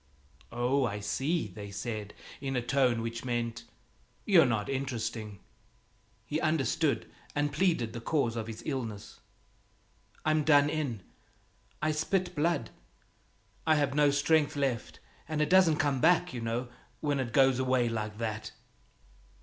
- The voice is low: Yes, low, 130 Hz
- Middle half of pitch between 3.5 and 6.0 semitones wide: Yes, average, 4.7 semitones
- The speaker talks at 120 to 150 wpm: Yes, average, 140 wpm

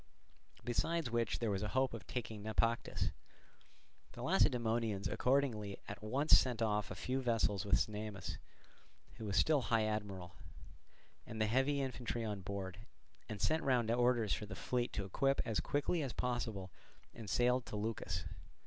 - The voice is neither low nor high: No, low, 115 Hz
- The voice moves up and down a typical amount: Yes, average, 3.3 semitones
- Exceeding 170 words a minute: No, average, 155 wpm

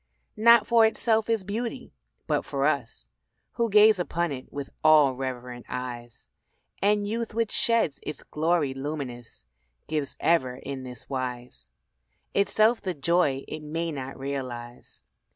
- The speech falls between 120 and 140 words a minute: Yes, slow, 135 wpm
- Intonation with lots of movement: Yes, wide, 8.1 semitones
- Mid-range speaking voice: Yes, medium, 150 Hz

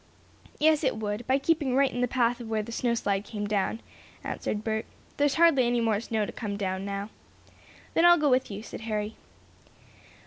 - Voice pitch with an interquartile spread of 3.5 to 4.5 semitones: Yes, average, 3.8 semitones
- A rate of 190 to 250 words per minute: Yes, average, 200 wpm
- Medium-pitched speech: No, high, 230 Hz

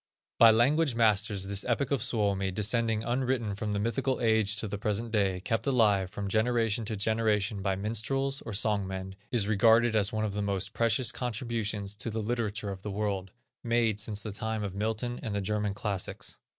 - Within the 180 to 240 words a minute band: Yes, average, 190 wpm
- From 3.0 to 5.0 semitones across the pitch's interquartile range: No, narrow, 2.4 semitones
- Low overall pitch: Yes, low, 110 Hz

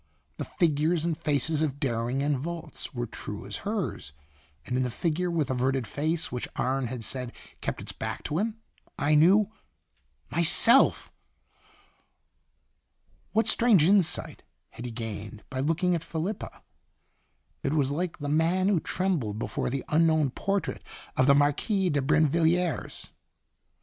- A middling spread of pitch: Yes, average, 4.7 semitones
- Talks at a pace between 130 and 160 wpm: Yes, average, 145 wpm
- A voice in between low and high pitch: Yes, medium, 155 Hz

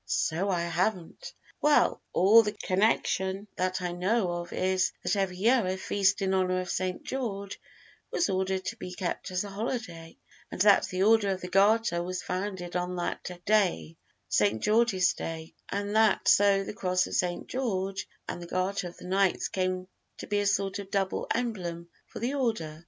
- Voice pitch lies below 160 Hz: No, high, 190 Hz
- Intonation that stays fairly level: Yes, narrow, 2.2 semitones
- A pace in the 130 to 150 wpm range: No, average, 185 wpm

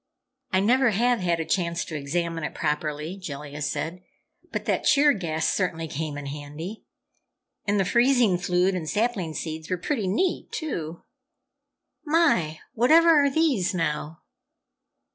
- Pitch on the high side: No, medium, 180 Hz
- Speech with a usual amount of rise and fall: No, wide, 7.1 semitones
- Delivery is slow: No, average, 145 wpm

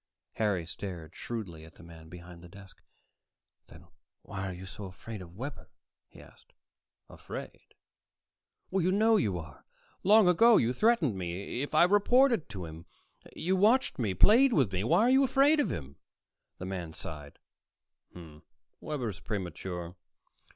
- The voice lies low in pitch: Yes, low, 100 Hz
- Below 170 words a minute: Yes, average, 150 wpm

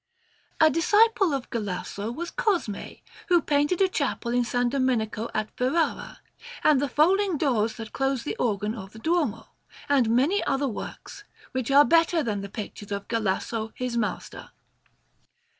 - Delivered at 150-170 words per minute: Yes, average, 155 wpm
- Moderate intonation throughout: No, wide, 6.4 semitones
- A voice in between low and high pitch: No, very high, 255 Hz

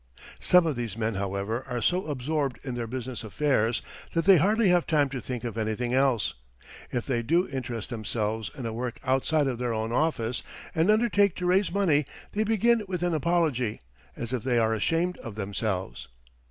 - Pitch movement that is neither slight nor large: No, wide, 6.5 semitones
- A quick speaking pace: No, average, 190 wpm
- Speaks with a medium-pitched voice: No, low, 130 Hz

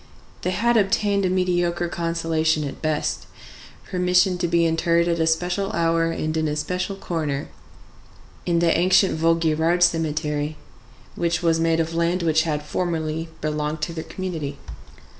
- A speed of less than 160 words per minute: Yes, average, 145 wpm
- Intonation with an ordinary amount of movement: No, narrow, 1.9 semitones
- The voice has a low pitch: No, medium, 165 Hz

